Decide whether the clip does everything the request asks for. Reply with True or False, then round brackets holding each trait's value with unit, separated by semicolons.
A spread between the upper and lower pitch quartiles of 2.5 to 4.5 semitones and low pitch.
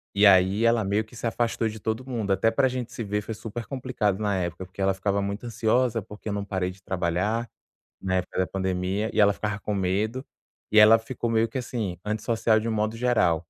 True (3.0 semitones; 105 Hz)